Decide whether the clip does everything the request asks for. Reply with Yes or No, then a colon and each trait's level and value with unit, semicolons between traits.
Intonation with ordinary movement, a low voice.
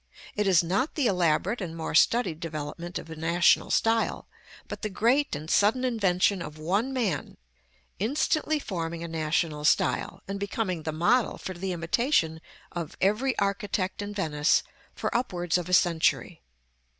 No: average, 4.7 semitones; medium, 185 Hz